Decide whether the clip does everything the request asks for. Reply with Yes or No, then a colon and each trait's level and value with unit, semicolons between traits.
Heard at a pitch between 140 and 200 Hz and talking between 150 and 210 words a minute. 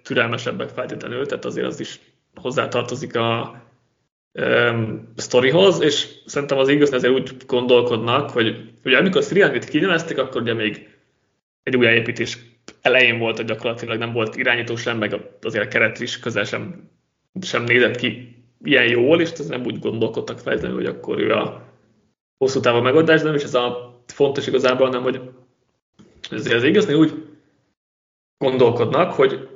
No: low, 125 Hz; fast, 155 wpm